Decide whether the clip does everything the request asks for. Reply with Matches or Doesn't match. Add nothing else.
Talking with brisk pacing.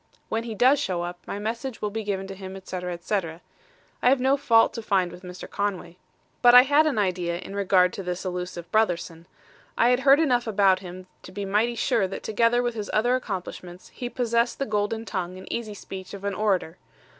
Matches